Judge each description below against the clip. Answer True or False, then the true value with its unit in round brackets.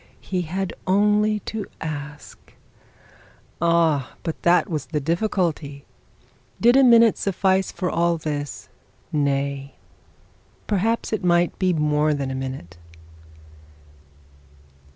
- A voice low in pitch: False (170 Hz)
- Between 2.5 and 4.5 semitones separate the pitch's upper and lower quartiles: False (5.0 semitones)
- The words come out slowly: True (110 wpm)